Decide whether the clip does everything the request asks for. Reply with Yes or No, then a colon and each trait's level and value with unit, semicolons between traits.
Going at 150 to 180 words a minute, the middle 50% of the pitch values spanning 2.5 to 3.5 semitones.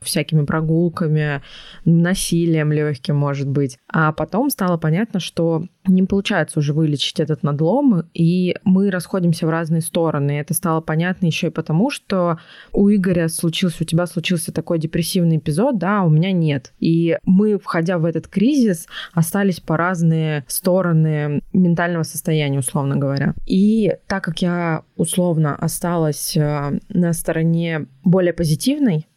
No: average, 140 wpm; average, 2.8 semitones